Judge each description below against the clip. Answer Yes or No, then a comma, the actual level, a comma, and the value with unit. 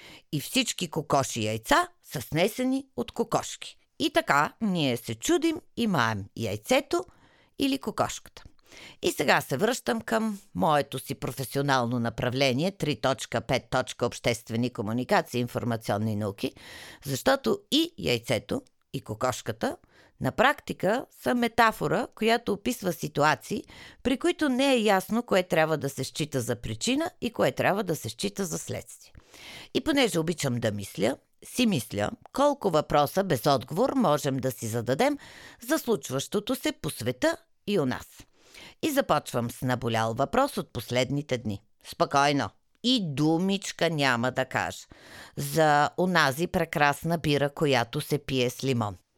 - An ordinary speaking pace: Yes, average, 135 wpm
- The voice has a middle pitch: Yes, medium, 150 Hz